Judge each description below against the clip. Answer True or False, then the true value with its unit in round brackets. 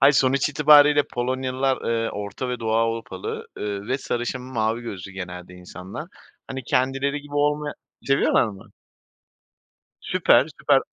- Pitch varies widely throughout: False (4.7 semitones)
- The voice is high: False (125 Hz)